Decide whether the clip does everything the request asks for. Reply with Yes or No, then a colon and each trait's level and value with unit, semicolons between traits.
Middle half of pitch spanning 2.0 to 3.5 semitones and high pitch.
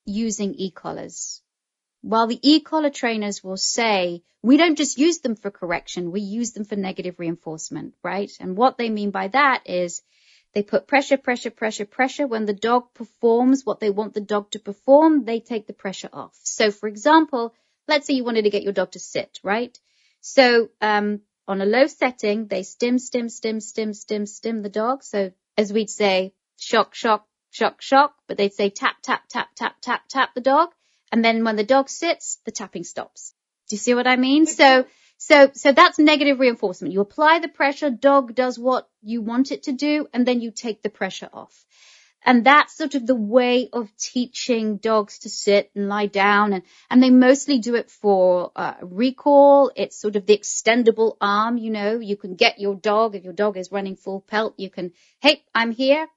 No: average, 4.2 semitones; high, 225 Hz